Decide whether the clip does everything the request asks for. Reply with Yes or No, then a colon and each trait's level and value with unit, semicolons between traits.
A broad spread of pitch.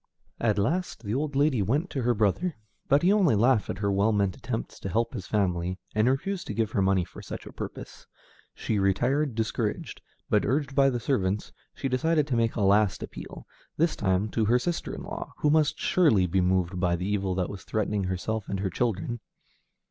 Yes: wide, 5.9 semitones